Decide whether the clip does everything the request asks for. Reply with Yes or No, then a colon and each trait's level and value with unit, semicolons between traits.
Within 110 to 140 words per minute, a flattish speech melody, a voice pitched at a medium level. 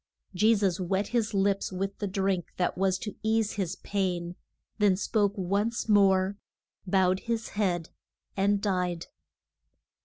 No: slow, 135 wpm; narrow, 1.9 semitones; high, 195 Hz